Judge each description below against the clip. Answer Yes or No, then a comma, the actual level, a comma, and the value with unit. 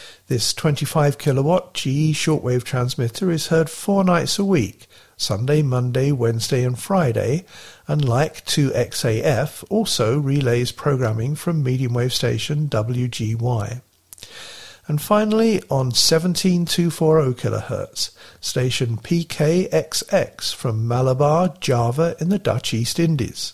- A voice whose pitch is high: No, medium, 140 Hz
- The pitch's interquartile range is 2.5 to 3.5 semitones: No, average, 4.9 semitones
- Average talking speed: No, slow, 110 wpm